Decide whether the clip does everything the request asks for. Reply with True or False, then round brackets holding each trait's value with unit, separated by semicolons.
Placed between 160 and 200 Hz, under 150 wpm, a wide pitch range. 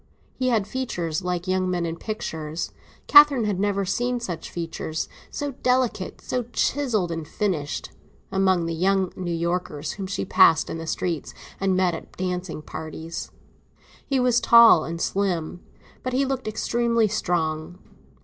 True (185 Hz; 140 wpm; 5.8 semitones)